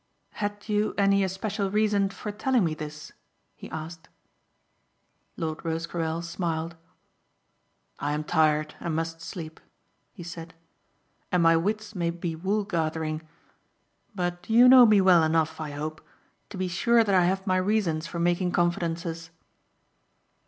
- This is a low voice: No, medium, 175 Hz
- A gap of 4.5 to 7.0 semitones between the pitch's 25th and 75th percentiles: No, average, 3.5 semitones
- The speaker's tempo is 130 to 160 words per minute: Yes, average, 140 wpm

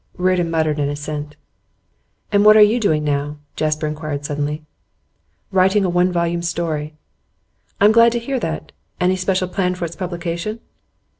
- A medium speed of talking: Yes, average, 155 wpm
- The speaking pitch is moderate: Yes, medium, 170 Hz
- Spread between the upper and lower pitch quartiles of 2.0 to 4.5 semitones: Yes, average, 3.8 semitones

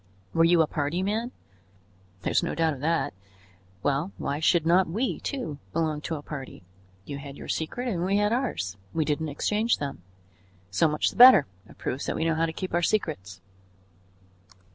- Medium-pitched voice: Yes, medium, 165 Hz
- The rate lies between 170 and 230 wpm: Yes, average, 190 wpm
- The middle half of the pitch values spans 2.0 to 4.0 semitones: No, average, 4.6 semitones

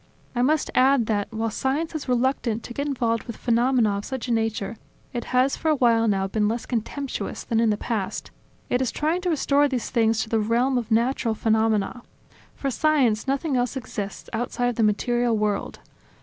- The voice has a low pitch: No, high, 240 Hz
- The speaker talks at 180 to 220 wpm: Yes, average, 195 wpm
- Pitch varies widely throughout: No, average, 3.1 semitones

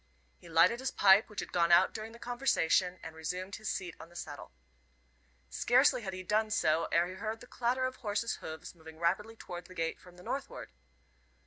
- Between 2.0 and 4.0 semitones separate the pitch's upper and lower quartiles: No, average, 4.9 semitones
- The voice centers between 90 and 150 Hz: No, high, 190 Hz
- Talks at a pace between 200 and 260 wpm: Yes, fast, 205 wpm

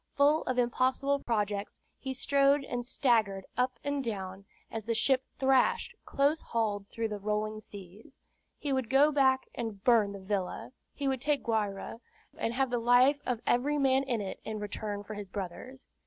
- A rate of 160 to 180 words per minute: Yes, average, 175 wpm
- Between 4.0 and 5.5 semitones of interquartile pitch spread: Yes, average, 4.4 semitones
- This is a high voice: Yes, high, 240 Hz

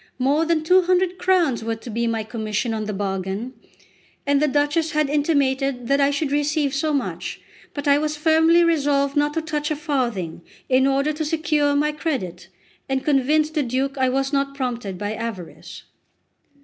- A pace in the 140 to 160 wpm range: No, average, 180 wpm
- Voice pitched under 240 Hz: No, very high, 280 Hz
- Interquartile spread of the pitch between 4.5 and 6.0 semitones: No, average, 3.7 semitones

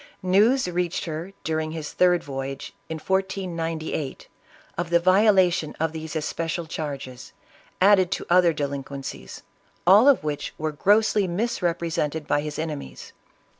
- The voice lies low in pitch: No, medium, 165 Hz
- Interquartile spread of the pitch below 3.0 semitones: No, average, 3.4 semitones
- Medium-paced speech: No, slow, 130 wpm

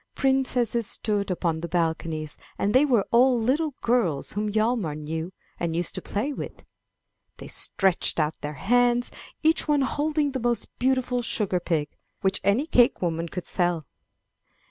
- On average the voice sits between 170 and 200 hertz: No, high, 210 Hz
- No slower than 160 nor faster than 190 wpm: No, average, 150 wpm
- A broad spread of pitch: Yes, wide, 6.8 semitones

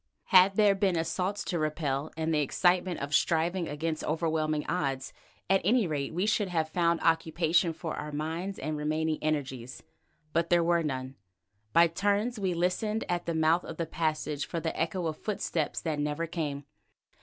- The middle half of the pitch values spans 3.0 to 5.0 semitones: No, narrow, 2.6 semitones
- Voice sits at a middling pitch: Yes, medium, 165 Hz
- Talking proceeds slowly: No, average, 175 wpm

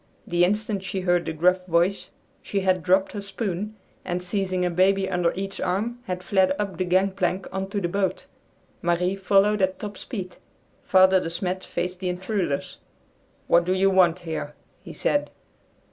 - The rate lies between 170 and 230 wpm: Yes, average, 175 wpm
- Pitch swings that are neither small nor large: No, narrow, 1.6 semitones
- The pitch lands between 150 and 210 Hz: Yes, medium, 185 Hz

